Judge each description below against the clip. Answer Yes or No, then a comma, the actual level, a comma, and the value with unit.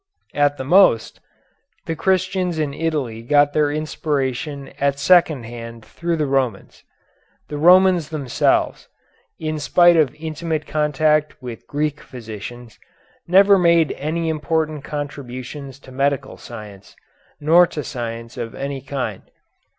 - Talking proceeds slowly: Yes, slow, 125 wpm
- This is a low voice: No, medium, 145 Hz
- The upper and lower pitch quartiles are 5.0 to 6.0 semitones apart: No, average, 3.8 semitones